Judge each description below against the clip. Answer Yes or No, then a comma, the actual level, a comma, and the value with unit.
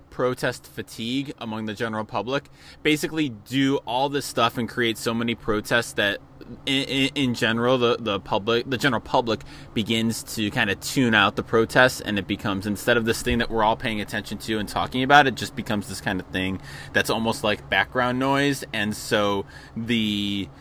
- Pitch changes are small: No, average, 3.2 semitones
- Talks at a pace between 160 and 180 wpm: No, average, 190 wpm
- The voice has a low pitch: Yes, low, 115 Hz